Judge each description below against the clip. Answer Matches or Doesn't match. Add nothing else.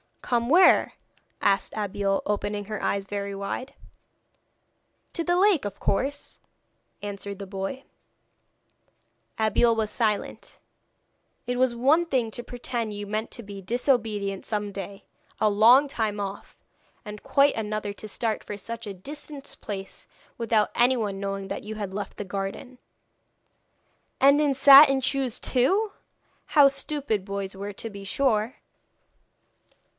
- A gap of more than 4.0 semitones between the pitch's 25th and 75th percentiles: Matches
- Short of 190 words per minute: Matches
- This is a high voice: Matches